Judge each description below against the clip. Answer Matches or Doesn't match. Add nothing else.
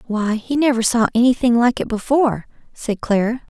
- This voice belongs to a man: Doesn't match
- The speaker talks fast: Doesn't match